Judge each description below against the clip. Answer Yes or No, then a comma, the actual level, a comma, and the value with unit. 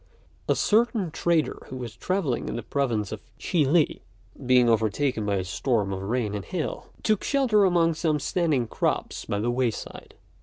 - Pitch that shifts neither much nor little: No, wide, 7.4 semitones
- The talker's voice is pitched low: Yes, low, 130 Hz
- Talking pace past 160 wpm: Yes, average, 180 wpm